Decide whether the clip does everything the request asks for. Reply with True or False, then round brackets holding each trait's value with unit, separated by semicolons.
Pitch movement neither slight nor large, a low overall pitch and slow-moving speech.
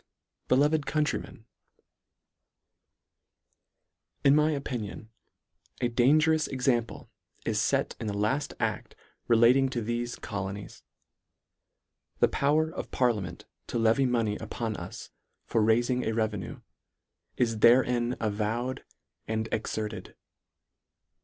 True (3.3 semitones; 120 Hz; 105 wpm)